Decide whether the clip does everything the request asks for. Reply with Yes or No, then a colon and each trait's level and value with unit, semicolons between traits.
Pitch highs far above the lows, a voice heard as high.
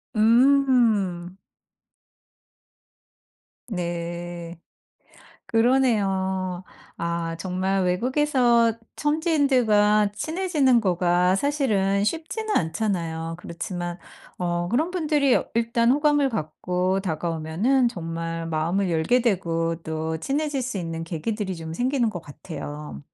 Yes: wide, 6.8 semitones; high, 195 Hz